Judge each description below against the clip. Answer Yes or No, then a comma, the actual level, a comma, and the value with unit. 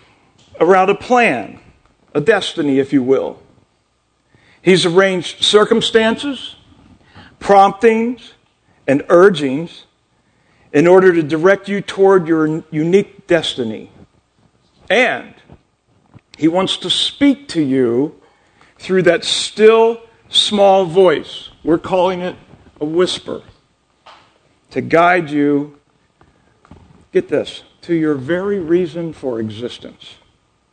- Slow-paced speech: Yes, slow, 100 wpm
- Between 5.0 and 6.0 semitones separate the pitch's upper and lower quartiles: No, average, 4.6 semitones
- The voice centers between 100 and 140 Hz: No, medium, 180 Hz